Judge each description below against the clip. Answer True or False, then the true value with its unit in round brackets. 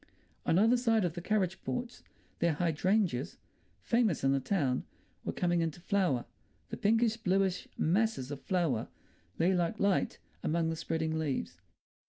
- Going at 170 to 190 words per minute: False (140 wpm)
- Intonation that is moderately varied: True (4.2 semitones)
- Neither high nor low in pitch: True (175 Hz)